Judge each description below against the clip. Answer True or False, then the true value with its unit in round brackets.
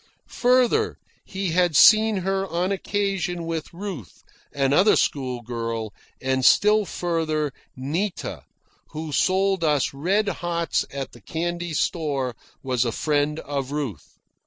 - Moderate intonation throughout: False (5.8 semitones)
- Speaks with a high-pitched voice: False (165 Hz)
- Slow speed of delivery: True (120 wpm)